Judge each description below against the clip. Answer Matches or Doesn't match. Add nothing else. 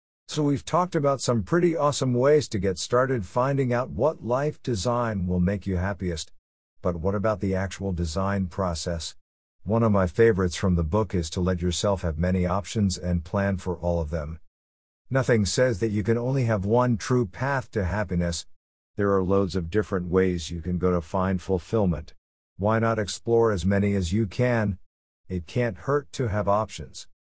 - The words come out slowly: Doesn't match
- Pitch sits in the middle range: Doesn't match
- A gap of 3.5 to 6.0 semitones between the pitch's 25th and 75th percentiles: Matches